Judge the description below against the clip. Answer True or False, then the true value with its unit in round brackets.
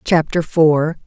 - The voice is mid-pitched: True (160 Hz)